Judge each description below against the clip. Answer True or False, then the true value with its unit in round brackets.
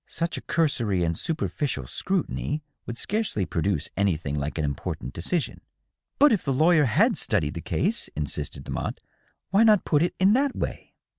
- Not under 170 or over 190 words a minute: True (180 wpm)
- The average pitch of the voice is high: False (140 Hz)